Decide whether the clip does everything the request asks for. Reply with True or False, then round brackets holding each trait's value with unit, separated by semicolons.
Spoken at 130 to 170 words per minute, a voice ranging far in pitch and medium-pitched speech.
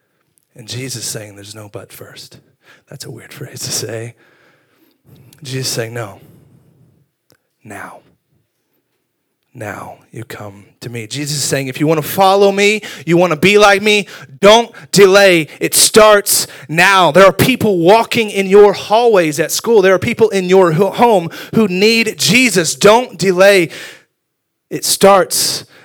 True (150 wpm; 6.3 semitones; 175 Hz)